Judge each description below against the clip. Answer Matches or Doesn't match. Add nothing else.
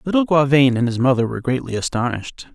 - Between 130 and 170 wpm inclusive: Doesn't match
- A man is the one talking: Matches